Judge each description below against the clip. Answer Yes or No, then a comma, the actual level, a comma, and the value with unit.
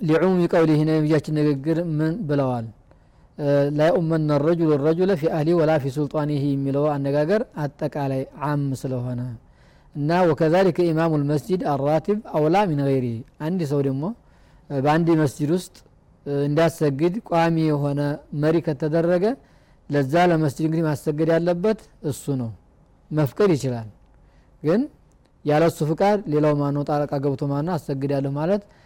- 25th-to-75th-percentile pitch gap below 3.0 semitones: Yes, narrow, 2.6 semitones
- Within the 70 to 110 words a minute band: No, fast, 120 wpm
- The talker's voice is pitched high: No, medium, 155 Hz